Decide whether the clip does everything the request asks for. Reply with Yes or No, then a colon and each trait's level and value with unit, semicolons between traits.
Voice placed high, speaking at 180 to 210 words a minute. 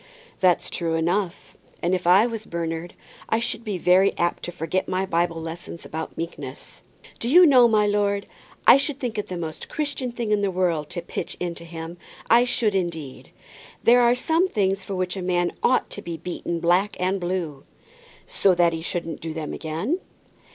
No: medium, 180 Hz; average, 190 wpm